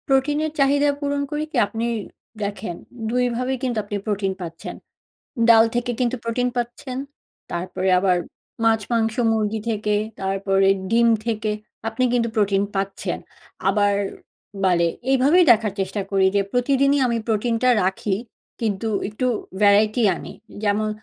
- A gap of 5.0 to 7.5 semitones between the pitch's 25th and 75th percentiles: No, average, 3.7 semitones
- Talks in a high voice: Yes, high, 225 Hz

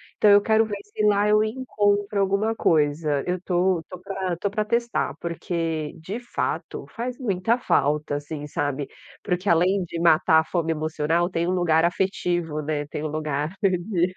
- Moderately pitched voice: Yes, medium, 180 Hz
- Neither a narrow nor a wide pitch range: Yes, average, 4.3 semitones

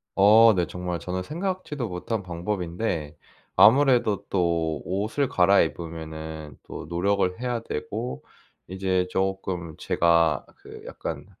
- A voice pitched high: No, very low, 90 Hz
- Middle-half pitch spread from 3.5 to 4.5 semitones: Yes, average, 4.2 semitones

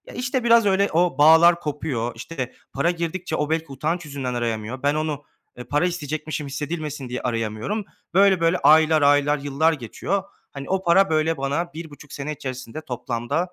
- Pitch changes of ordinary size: Yes, average, 3.8 semitones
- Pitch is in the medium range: Yes, medium, 155 Hz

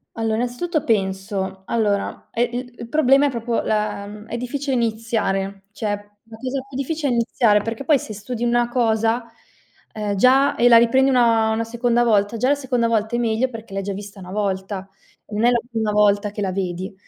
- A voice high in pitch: Yes, high, 225 Hz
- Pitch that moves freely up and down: No, average, 2.9 semitones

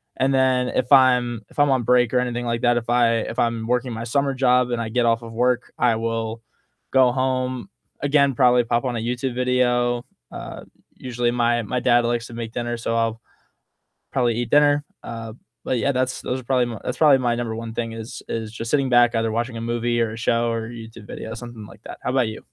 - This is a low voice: Yes, low, 120 Hz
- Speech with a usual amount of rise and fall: No, narrow, 1.6 semitones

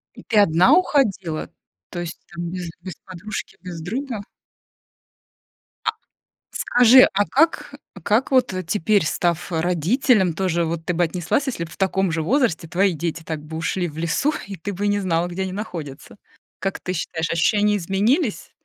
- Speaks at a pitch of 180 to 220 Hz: Yes, medium, 185 Hz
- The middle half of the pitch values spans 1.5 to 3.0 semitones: No, average, 3.8 semitones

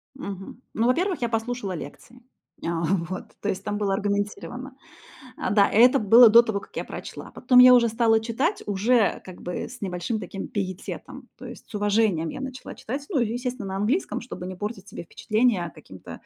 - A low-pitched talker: No, high, 220 Hz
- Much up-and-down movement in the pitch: No, average, 4.2 semitones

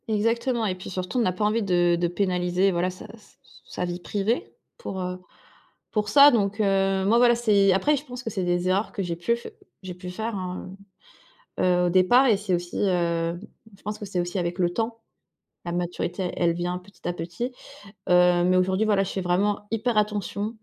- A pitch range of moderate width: Yes, average, 3.3 semitones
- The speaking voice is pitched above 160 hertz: Yes, high, 190 Hz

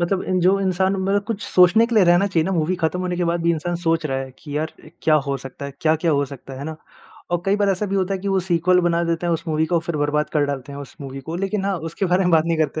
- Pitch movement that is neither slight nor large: Yes, average, 3.3 semitones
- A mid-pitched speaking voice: Yes, medium, 170 Hz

